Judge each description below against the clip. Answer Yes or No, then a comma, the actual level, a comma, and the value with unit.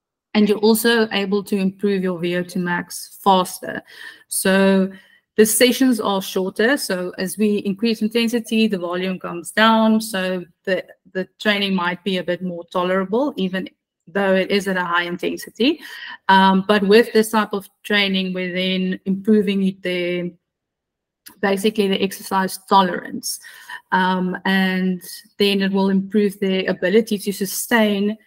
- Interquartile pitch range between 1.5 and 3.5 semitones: Yes, narrow, 2.6 semitones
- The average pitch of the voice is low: No, high, 195 Hz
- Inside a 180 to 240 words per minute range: No, average, 140 wpm